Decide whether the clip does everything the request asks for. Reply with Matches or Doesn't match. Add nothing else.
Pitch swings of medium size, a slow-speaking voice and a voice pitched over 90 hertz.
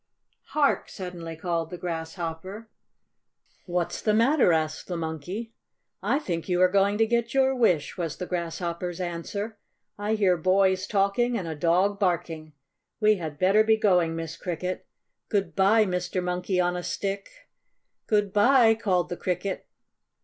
Doesn't match